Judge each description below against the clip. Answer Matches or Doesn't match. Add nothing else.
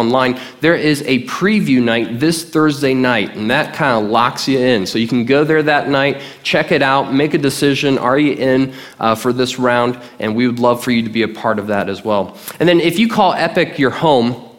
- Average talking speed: Doesn't match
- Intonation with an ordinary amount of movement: Matches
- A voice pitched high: Doesn't match